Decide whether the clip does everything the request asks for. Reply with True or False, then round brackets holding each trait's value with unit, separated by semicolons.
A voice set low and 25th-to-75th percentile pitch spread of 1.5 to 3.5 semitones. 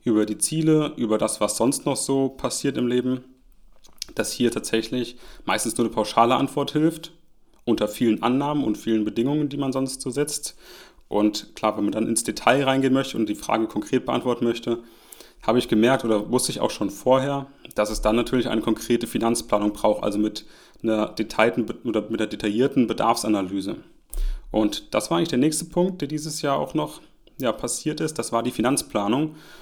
False (120 Hz; 3.9 semitones)